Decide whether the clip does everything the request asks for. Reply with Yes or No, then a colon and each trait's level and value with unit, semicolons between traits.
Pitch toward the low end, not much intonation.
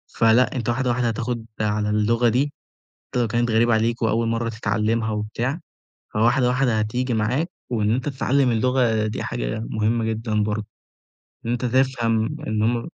Yes: low, 115 Hz; narrow, 2.3 semitones